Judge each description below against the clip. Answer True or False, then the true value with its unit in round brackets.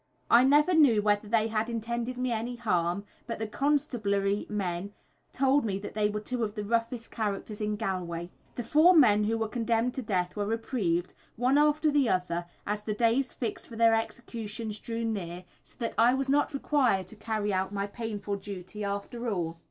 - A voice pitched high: True (220 Hz)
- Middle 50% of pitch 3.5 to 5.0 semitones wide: False (3.1 semitones)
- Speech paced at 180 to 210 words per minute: True (190 wpm)